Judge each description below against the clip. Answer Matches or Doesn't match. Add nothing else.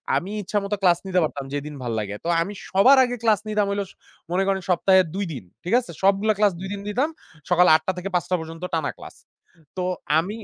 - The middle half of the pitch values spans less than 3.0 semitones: Doesn't match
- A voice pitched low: Doesn't match